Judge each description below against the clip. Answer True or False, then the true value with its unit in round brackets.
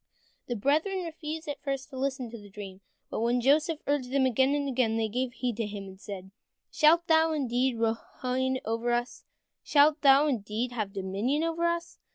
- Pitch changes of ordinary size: True (4.5 semitones)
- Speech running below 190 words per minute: False (200 wpm)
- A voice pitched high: True (260 Hz)